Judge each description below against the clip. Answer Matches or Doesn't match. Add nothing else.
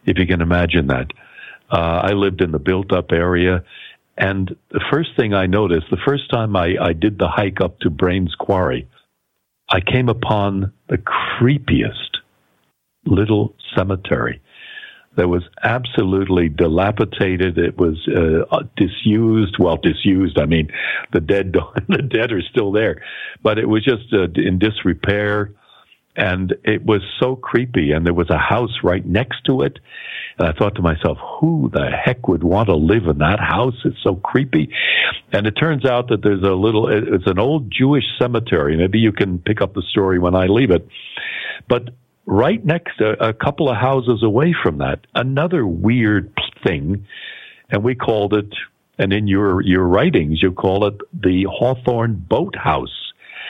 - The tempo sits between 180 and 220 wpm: Doesn't match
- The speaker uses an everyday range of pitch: Matches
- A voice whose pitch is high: Doesn't match